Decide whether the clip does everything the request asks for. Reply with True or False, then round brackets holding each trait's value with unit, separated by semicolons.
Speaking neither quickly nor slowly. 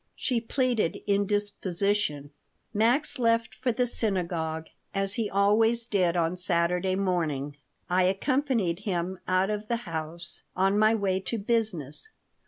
False (130 wpm)